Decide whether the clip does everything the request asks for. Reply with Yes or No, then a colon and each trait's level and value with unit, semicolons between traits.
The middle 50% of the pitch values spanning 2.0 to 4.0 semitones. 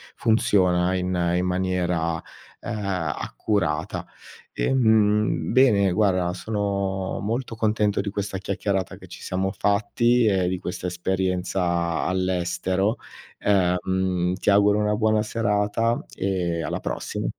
Yes: narrow, 2.5 semitones